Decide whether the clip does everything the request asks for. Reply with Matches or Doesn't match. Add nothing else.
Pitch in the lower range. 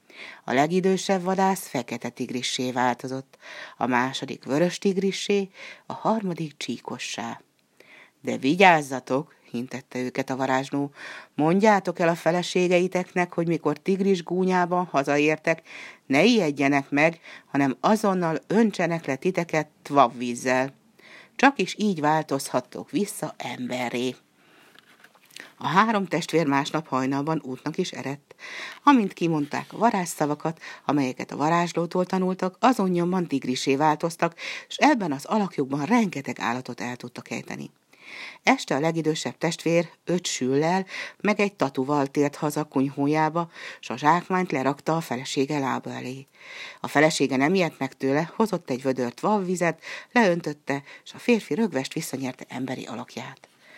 Doesn't match